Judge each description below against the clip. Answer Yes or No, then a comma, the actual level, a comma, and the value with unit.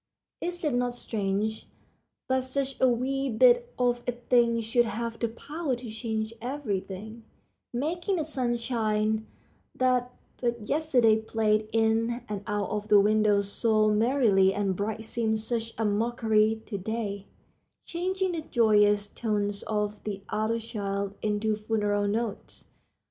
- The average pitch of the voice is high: Yes, high, 225 Hz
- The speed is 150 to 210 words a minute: No, average, 140 wpm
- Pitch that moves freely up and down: No, average, 2.7 semitones